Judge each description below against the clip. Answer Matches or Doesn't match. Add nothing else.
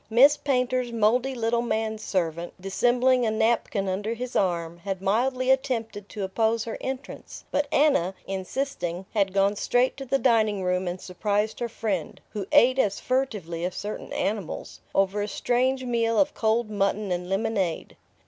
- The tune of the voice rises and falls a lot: Doesn't match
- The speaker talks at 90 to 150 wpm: Doesn't match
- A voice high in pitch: Matches